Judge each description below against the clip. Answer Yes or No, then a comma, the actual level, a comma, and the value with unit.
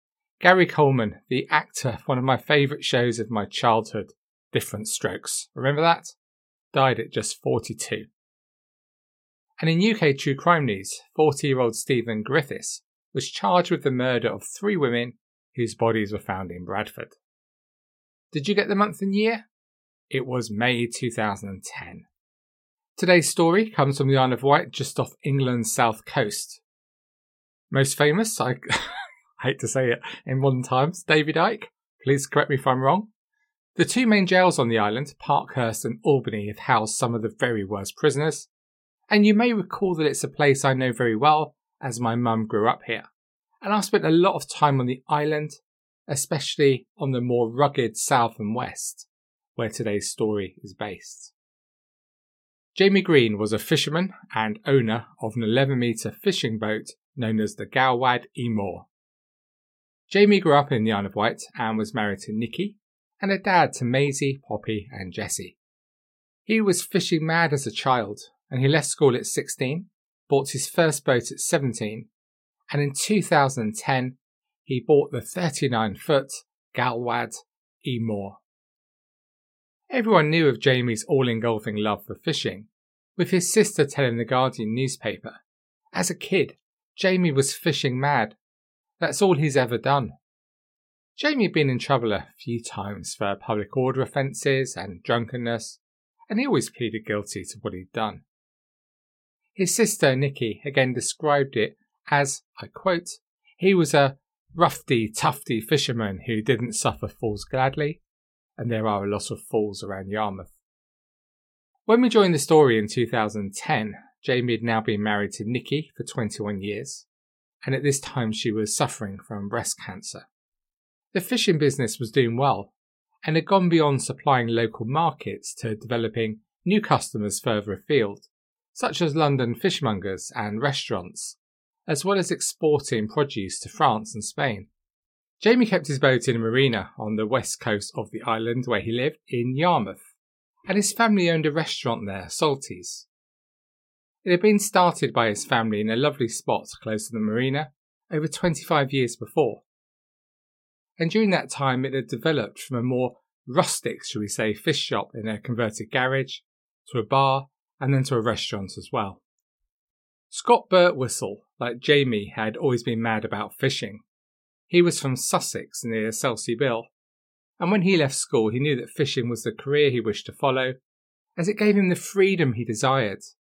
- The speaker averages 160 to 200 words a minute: Yes, average, 165 wpm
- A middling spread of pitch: No, wide, 6.3 semitones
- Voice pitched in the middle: No, low, 130 Hz